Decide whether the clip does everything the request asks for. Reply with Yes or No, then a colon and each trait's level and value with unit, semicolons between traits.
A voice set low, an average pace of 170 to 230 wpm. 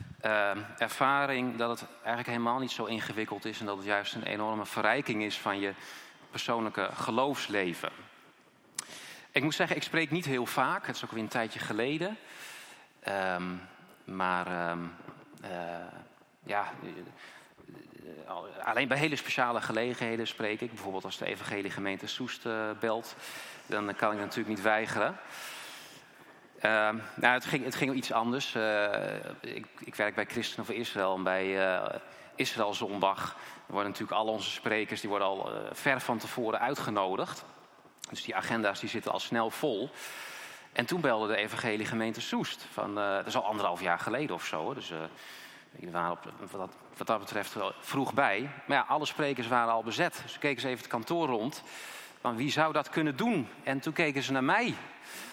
Yes: low, 115 Hz; average, 175 wpm